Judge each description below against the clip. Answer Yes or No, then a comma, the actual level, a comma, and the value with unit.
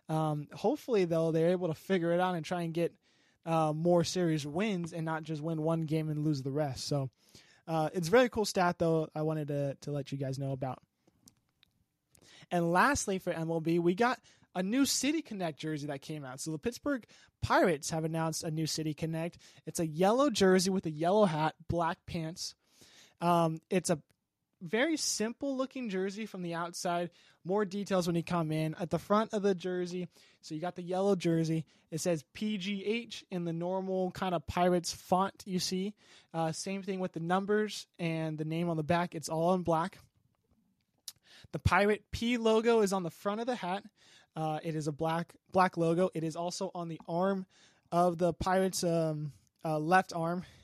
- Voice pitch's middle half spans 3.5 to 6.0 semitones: No, average, 3.0 semitones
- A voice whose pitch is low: No, medium, 175 Hz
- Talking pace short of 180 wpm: No, average, 195 wpm